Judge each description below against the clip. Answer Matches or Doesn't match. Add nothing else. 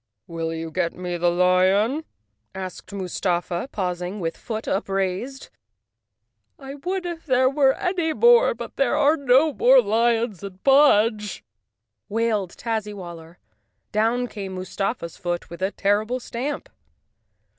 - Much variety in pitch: Matches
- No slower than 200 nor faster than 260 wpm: Doesn't match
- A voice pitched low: Doesn't match